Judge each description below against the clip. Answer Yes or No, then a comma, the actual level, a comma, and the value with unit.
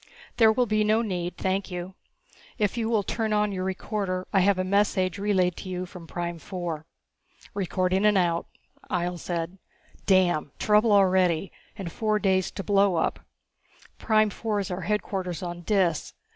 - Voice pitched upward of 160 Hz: Yes, high, 190 Hz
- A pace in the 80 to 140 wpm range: No, average, 160 wpm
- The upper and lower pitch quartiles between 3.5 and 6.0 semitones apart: No, average, 2.7 semitones